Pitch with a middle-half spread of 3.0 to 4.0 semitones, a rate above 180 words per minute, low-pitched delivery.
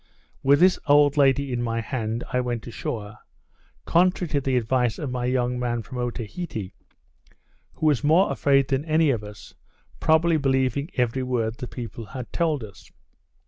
No: average, 3.5 semitones; average, 165 wpm; low, 130 Hz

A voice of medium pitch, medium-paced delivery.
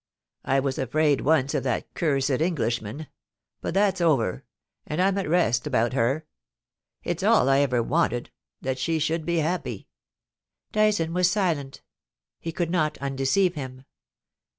Yes: medium, 150 Hz; average, 150 wpm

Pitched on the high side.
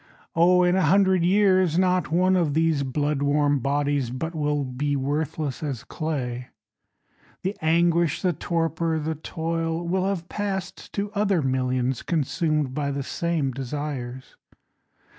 No: medium, 160 Hz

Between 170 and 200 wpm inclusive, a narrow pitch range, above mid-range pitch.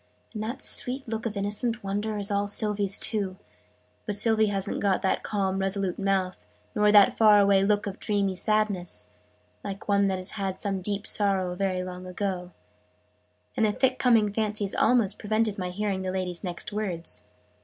Yes: average, 175 wpm; narrow, 2.0 semitones; high, 200 Hz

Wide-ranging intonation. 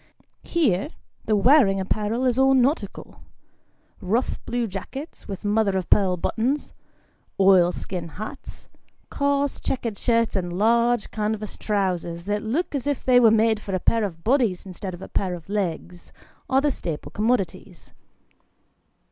No: average, 4.6 semitones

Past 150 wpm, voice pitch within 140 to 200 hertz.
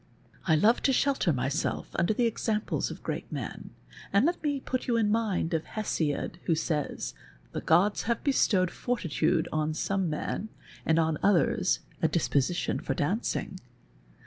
Yes: average, 160 wpm; medium, 185 Hz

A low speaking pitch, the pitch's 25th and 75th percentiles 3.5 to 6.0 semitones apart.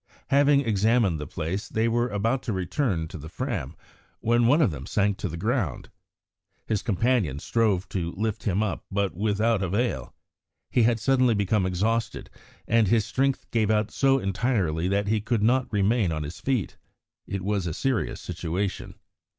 Yes: low, 105 Hz; average, 4.1 semitones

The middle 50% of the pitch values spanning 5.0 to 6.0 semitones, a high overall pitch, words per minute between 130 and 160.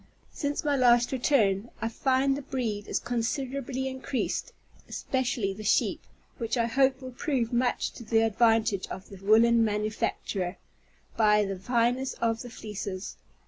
No: average, 3.5 semitones; high, 235 Hz; average, 145 wpm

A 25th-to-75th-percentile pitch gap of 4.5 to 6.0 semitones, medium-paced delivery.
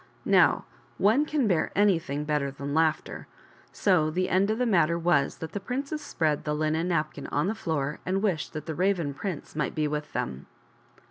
Yes: average, 4.8 semitones; average, 190 wpm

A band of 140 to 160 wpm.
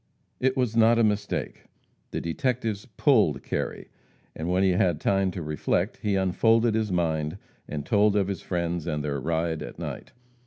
No: average, 170 wpm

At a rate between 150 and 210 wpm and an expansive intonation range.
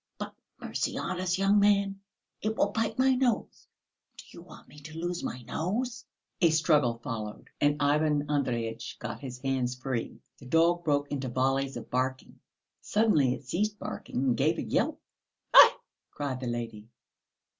Yes: average, 165 wpm; wide, 6.5 semitones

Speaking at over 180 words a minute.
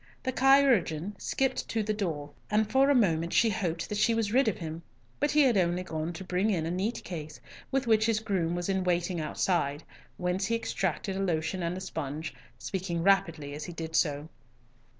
Yes: average, 200 wpm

